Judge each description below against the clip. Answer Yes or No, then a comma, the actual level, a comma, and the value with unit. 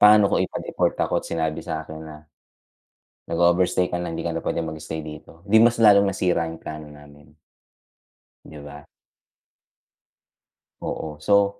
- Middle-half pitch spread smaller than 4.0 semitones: Yes, average, 3.5 semitones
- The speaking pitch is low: Yes, very low, 80 Hz